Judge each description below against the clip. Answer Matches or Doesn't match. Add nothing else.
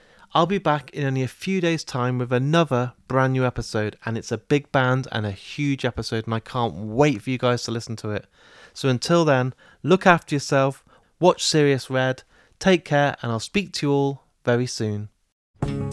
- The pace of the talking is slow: Doesn't match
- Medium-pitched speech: Doesn't match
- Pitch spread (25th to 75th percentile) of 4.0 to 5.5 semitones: Matches